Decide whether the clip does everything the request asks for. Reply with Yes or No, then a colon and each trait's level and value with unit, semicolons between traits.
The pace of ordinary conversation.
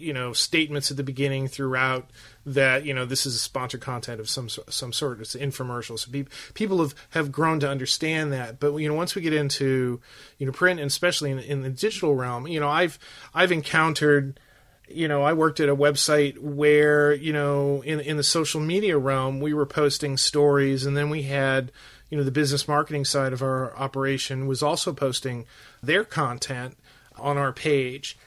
Yes: average, 195 wpm